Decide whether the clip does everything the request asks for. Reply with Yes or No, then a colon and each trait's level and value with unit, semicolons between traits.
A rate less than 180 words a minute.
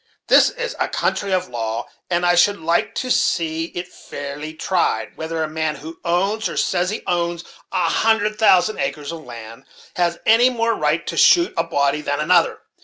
No: average, 185 wpm